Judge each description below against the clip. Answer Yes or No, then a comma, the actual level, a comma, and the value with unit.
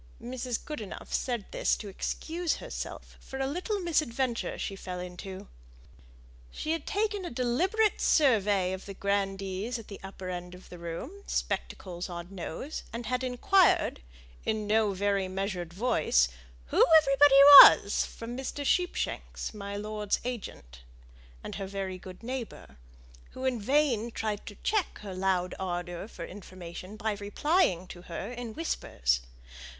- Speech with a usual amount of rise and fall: No, wide, 5.8 semitones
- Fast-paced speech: No, average, 145 wpm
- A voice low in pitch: No, high, 210 Hz